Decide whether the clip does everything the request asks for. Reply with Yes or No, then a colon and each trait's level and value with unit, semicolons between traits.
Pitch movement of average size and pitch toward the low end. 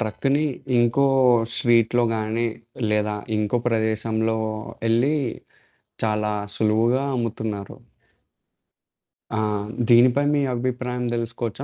No: narrow, 2.1 semitones; low, 115 Hz